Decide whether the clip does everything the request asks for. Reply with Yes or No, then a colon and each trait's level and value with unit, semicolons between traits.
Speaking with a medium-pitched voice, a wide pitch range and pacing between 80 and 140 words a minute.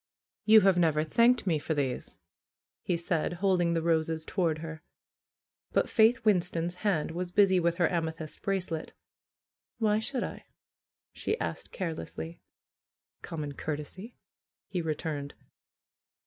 No: medium, 170 Hz; average, 3.5 semitones; slow, 135 wpm